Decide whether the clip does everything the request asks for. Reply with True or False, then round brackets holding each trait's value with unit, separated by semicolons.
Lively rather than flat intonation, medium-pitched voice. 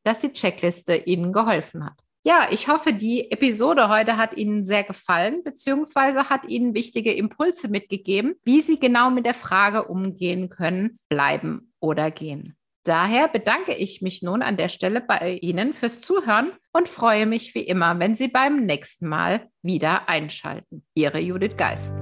False (5.8 semitones; 210 Hz)